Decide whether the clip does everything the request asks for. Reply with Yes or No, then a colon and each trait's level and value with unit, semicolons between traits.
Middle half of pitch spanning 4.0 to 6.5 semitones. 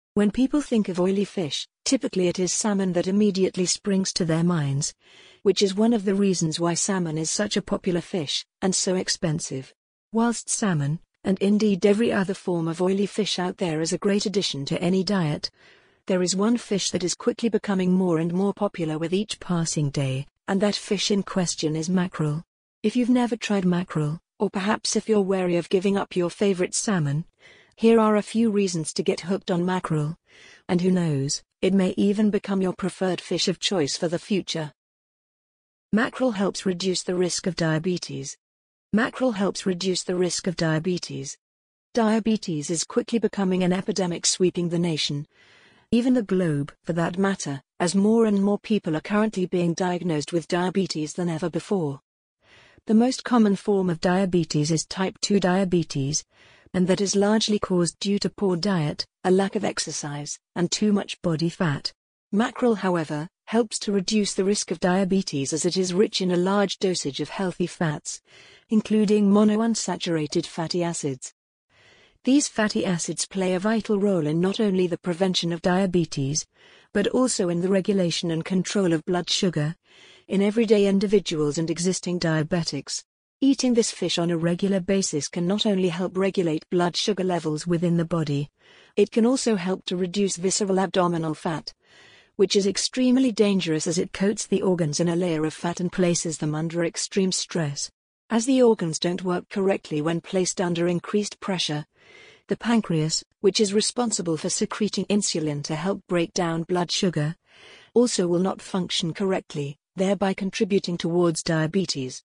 No: average, 3.1 semitones